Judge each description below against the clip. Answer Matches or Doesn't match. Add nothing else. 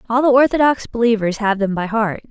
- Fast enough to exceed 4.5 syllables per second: Matches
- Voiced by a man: Doesn't match